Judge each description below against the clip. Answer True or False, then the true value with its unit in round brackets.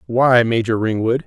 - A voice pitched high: False (120 Hz)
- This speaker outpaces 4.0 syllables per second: True (4.5 syllables/s)